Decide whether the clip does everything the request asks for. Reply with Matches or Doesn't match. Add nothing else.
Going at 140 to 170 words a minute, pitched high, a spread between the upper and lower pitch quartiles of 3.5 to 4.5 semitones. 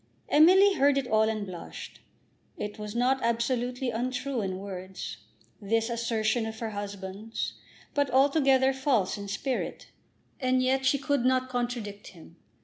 Matches